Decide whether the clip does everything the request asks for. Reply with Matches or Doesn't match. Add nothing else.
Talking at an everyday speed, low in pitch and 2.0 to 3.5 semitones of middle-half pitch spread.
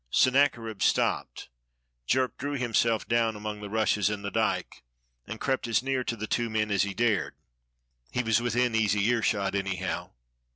Matches